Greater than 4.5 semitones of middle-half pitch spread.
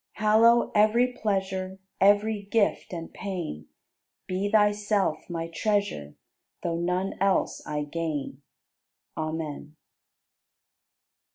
No: average, 4.0 semitones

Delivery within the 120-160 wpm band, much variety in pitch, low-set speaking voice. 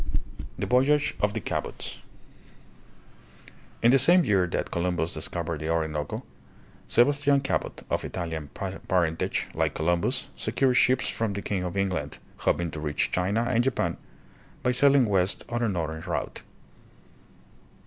Yes: average, 140 wpm; wide, 6.9 semitones; very low, 95 Hz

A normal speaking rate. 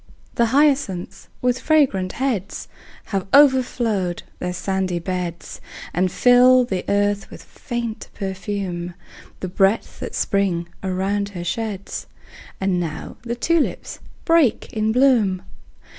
No: slow, 115 wpm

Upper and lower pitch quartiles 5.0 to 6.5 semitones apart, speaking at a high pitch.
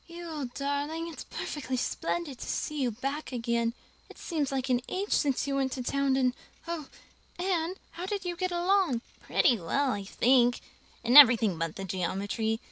Yes: wide, 5.5 semitones; very high, 275 Hz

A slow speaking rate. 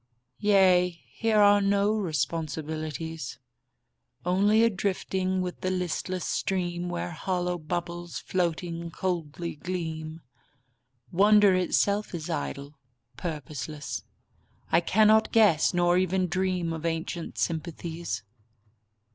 Yes: slow, 100 wpm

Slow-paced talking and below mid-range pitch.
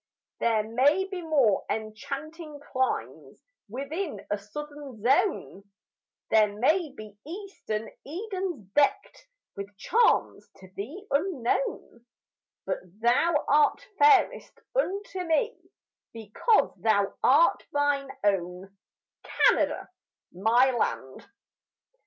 No: slow, 95 wpm; very high, 275 Hz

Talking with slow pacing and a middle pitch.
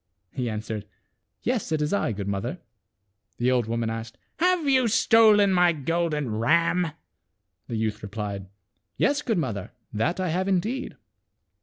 No: average, 165 wpm; medium, 150 Hz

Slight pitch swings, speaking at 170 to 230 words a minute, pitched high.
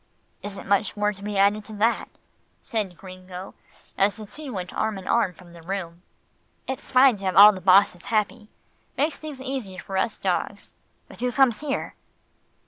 No: average, 3.6 semitones; average, 180 wpm; high, 205 Hz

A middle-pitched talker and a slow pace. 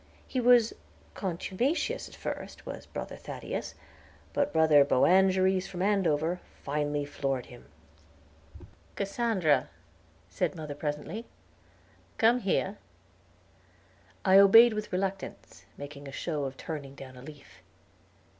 Yes: medium, 175 Hz; slow, 110 wpm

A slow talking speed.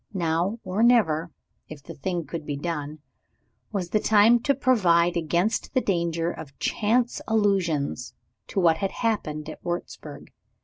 No: average, 145 wpm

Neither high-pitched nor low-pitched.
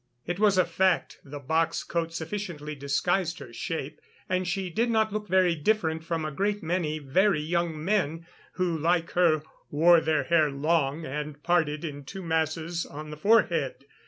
Yes: medium, 165 Hz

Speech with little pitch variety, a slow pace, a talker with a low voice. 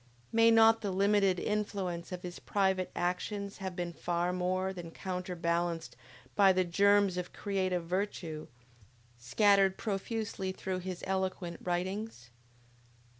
No: narrow, 2.2 semitones; slow, 125 wpm; medium, 185 Hz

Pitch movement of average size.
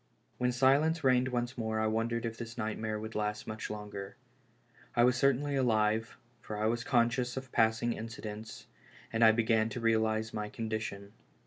No: narrow, 2.0 semitones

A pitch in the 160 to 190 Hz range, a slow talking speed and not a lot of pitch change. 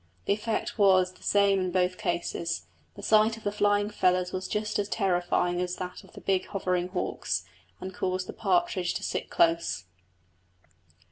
No: medium, 185 Hz; average, 175 wpm; narrow, 2.2 semitones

